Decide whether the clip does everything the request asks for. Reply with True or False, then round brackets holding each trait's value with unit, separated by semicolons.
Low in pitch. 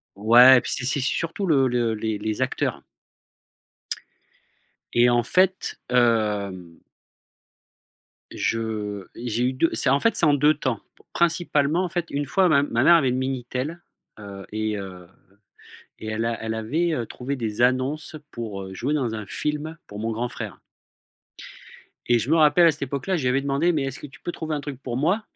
True (130 Hz)